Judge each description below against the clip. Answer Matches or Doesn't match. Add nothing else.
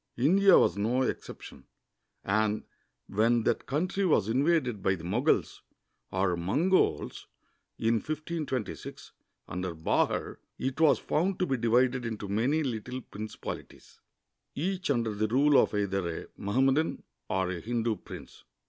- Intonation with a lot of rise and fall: Matches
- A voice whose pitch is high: Doesn't match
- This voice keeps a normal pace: Doesn't match